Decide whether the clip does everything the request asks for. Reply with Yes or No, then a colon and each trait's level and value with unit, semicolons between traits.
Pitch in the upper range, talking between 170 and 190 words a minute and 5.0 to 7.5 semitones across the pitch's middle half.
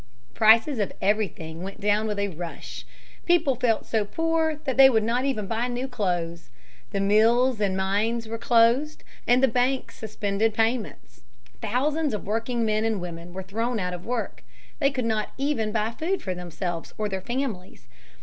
No: high, 220 Hz; average, 175 wpm; average, 4.1 semitones